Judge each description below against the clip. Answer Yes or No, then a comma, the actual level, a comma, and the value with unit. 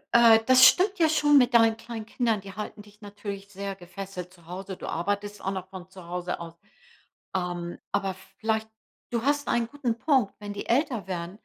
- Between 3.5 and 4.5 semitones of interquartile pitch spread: Yes, average, 3.8 semitones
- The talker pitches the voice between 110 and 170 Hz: No, high, 205 Hz